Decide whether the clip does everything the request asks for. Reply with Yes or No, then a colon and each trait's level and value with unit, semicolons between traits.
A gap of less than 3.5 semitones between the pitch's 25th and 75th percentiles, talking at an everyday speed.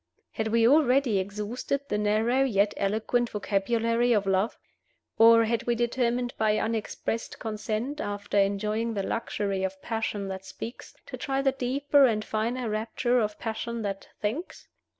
Yes: narrow, 2.6 semitones; average, 150 wpm